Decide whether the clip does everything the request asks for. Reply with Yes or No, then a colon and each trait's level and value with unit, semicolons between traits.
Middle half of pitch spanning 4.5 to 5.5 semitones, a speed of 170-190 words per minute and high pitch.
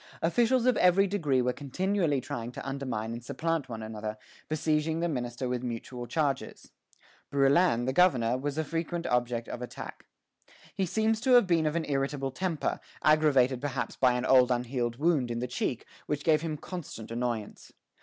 No: average, 5.1 semitones; average, 175 wpm; medium, 140 Hz